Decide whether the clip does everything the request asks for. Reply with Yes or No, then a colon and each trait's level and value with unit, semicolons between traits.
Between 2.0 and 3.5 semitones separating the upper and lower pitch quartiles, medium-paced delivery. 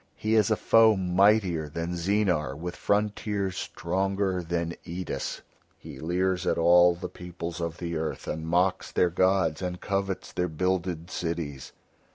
Yes: narrow, 2.4 semitones; average, 150 wpm